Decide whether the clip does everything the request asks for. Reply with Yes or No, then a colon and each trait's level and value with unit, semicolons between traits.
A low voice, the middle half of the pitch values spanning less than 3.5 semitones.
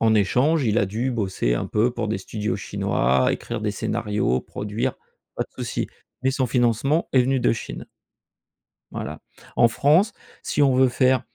No: low, 120 Hz; average, 3.8 semitones